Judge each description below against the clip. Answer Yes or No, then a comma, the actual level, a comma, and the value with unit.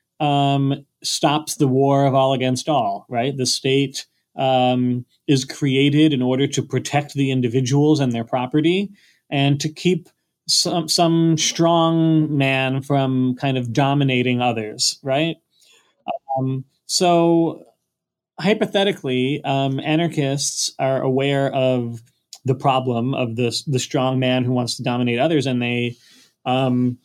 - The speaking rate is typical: No, slow, 130 wpm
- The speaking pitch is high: No, low, 135 Hz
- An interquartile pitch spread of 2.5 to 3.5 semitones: Yes, average, 3.2 semitones